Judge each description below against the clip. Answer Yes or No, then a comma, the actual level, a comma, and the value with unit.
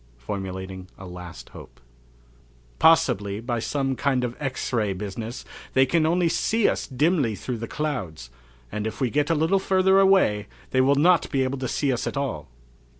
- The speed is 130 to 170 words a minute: No, average, 180 wpm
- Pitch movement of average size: No, wide, 6.8 semitones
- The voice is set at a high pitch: No, low, 130 Hz